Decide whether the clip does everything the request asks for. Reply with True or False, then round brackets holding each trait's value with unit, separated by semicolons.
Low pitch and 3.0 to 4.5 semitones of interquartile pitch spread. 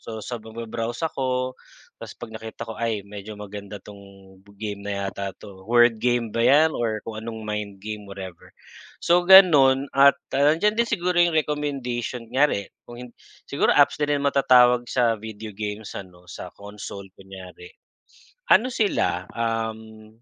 True (110 Hz; 4.2 semitones)